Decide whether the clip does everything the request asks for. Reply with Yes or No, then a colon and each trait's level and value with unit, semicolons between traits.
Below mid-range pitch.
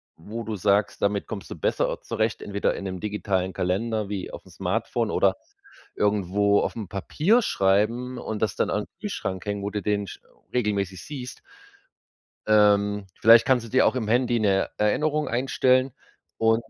Yes: low, 105 Hz